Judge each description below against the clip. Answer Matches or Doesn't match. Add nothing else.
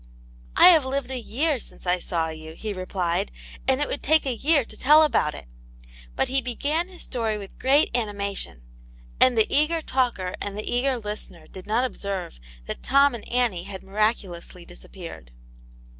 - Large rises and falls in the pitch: Matches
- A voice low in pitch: Doesn't match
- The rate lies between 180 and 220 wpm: Matches